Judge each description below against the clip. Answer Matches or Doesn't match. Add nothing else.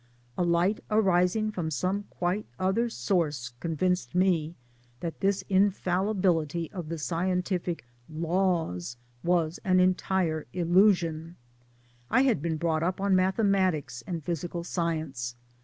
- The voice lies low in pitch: Doesn't match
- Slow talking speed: Matches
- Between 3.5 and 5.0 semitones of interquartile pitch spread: Doesn't match